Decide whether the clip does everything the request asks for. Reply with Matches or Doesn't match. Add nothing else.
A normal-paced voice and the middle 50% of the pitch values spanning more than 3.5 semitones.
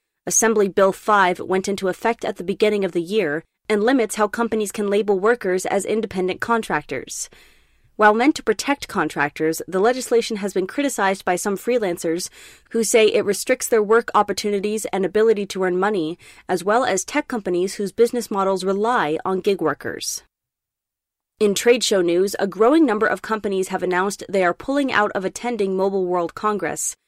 Doesn't match